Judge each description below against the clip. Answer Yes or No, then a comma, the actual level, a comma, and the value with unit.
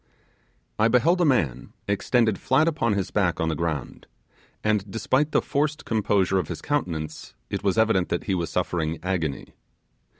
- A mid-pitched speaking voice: No, low, 100 Hz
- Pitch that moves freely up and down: Yes, wide, 6.1 semitones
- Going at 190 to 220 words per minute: No, average, 165 wpm